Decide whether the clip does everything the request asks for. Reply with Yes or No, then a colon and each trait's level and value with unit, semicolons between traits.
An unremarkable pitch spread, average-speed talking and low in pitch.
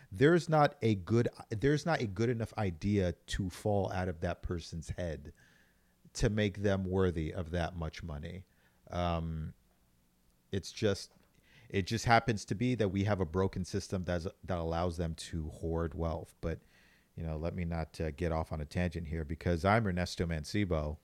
Yes: average, 3.8 semitones; average, 180 wpm; very low, 90 Hz